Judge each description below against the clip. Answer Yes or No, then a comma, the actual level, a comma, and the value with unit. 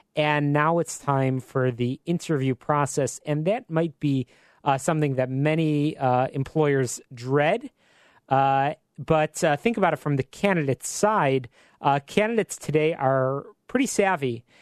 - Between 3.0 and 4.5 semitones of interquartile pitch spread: Yes, average, 3.5 semitones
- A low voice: No, medium, 145 Hz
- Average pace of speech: Yes, average, 145 wpm